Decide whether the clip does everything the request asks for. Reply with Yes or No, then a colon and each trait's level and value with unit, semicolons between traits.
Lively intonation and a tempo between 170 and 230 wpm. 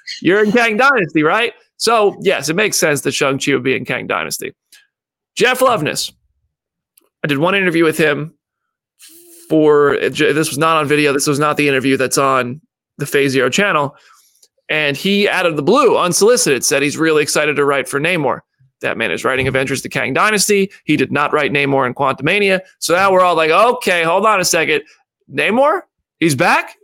Yes: wide, 6.3 semitones; average, 190 wpm